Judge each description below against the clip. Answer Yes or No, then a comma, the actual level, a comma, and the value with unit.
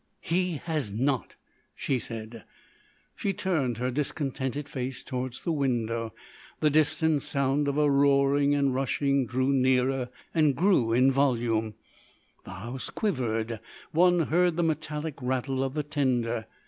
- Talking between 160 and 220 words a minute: No, slow, 135 wpm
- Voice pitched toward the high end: No, low, 135 Hz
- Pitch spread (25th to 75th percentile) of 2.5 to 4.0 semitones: Yes, average, 3.2 semitones